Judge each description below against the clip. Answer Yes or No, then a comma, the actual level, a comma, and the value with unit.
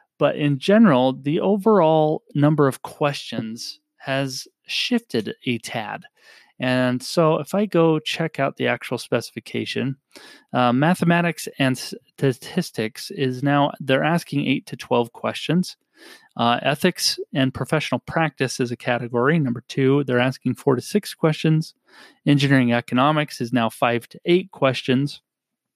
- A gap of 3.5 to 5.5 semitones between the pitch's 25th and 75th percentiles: Yes, average, 4.1 semitones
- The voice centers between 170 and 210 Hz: No, medium, 140 Hz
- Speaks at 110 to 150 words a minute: Yes, slow, 135 wpm